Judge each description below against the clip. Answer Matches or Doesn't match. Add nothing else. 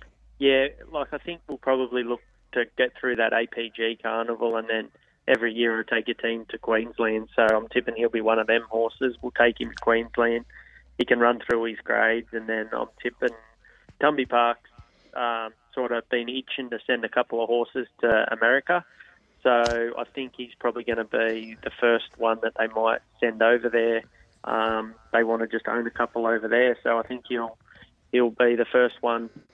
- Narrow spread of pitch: Matches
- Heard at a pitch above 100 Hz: Matches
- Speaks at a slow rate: Doesn't match